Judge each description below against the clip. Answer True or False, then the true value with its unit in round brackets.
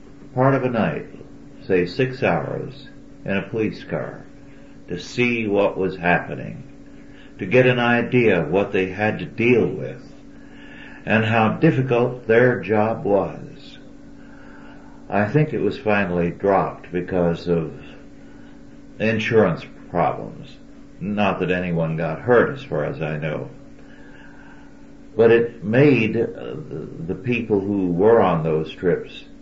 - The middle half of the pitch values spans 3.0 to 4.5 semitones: False (5.6 semitones)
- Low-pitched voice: True (110 Hz)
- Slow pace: True (130 wpm)